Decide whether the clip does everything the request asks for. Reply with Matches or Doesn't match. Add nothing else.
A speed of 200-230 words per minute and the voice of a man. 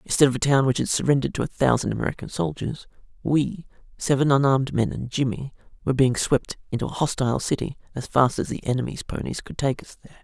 Matches